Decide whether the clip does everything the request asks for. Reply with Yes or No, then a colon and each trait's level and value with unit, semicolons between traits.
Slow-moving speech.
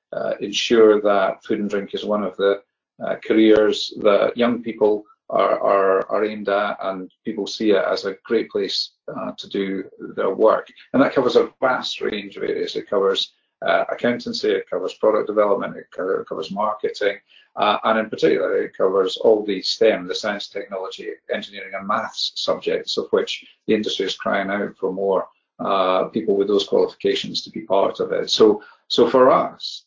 No: average, 185 wpm